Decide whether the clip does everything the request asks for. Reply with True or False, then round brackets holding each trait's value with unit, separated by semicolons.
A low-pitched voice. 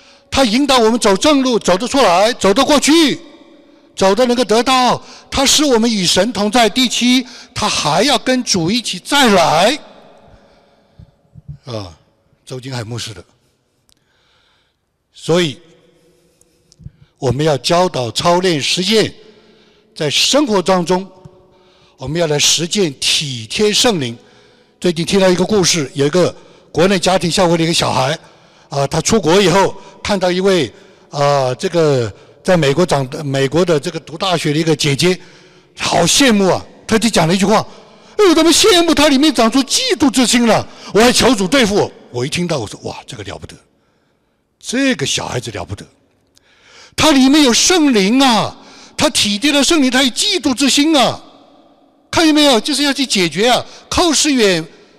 False (190 Hz)